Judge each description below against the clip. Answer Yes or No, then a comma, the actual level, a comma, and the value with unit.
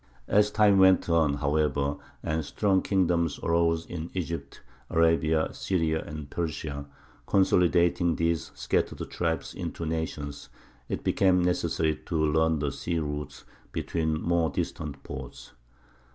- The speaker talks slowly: Yes, slow, 125 wpm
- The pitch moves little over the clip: Yes, narrow, 2.1 semitones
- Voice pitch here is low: Yes, very low, 80 Hz